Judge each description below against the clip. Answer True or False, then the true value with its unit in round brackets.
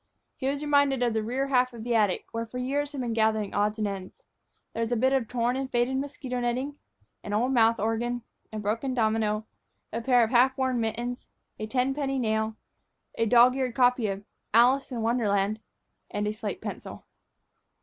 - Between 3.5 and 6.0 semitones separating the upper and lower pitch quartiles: False (3.0 semitones)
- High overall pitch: True (240 Hz)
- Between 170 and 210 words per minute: True (195 wpm)